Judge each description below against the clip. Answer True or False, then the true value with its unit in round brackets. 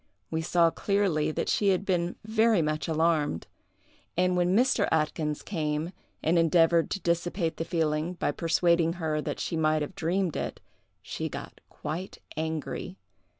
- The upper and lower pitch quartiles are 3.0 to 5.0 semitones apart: False (2.5 semitones)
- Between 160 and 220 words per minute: False (150 wpm)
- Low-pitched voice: False (165 Hz)